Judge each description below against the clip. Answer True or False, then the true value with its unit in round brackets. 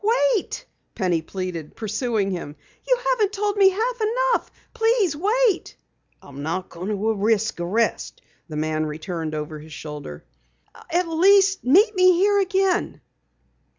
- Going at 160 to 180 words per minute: False (135 wpm)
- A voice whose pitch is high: True (255 Hz)